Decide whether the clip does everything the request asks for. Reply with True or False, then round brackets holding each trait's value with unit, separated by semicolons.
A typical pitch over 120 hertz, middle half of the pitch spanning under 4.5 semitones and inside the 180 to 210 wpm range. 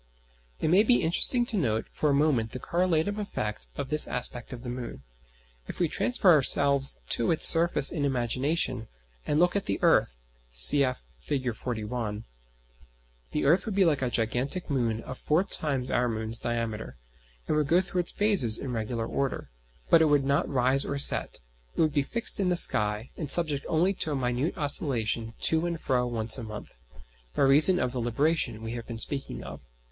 False (135 Hz; 5.5 semitones; 190 wpm)